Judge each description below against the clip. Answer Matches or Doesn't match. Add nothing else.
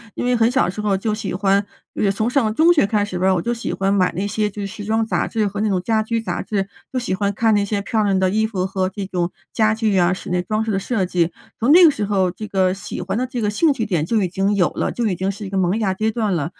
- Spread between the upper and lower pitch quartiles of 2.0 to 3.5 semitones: Matches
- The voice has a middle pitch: Doesn't match